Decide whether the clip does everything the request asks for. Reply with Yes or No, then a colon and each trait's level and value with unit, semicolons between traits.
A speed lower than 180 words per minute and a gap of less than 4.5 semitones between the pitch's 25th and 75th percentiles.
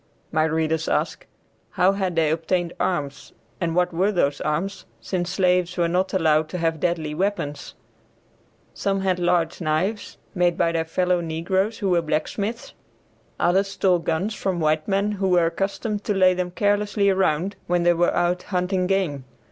Yes: average, 165 wpm; average, 2.9 semitones